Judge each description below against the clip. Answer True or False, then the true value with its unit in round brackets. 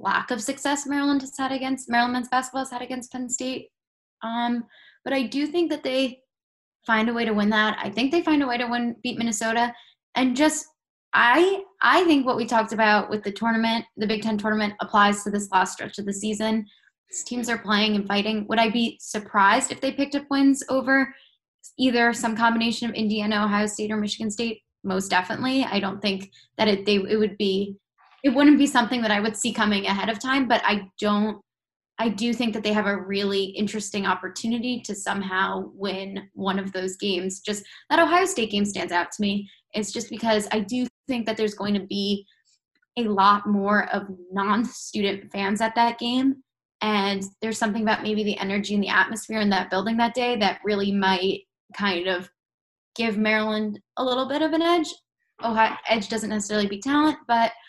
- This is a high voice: True (220 Hz)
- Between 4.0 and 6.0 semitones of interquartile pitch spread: False (3.6 semitones)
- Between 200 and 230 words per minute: True (205 wpm)